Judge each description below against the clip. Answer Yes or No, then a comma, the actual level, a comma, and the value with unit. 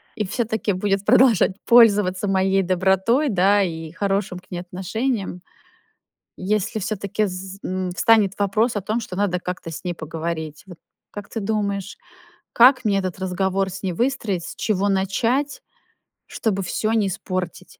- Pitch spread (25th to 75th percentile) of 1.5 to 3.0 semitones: Yes, average, 2.7 semitones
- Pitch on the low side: No, high, 195 Hz